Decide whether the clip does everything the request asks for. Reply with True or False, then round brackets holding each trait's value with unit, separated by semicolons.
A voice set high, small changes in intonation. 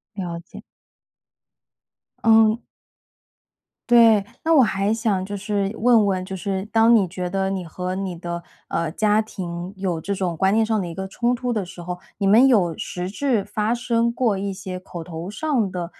False (195 Hz; 3.5 semitones)